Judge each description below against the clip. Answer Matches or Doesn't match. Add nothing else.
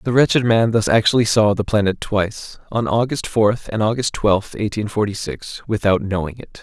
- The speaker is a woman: Doesn't match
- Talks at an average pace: Matches